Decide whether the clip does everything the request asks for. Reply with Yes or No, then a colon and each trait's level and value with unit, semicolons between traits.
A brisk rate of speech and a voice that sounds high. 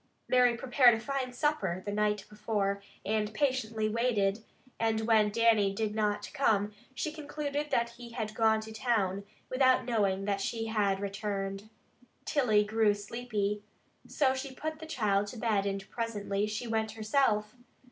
No: average, 155 wpm; high, 220 Hz